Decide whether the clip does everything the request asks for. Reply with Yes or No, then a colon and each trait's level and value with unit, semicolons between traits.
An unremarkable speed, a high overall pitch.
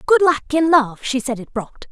No: fast, 250 wpm; very high, 280 Hz